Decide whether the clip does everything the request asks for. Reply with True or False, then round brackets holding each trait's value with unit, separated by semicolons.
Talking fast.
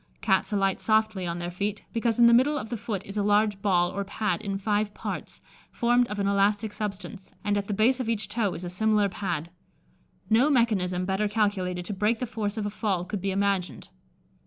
True (215 wpm)